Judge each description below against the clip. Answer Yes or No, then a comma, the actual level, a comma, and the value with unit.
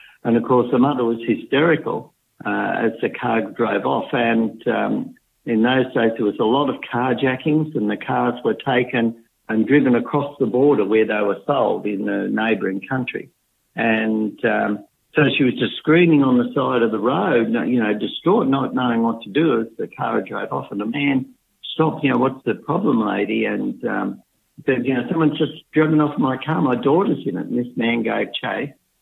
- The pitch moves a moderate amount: Yes, average, 3.8 semitones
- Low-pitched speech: Yes, low, 125 Hz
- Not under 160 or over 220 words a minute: Yes, fast, 205 wpm